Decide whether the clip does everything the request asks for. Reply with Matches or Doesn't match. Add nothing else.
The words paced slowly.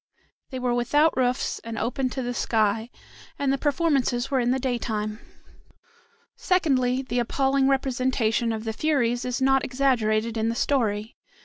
Doesn't match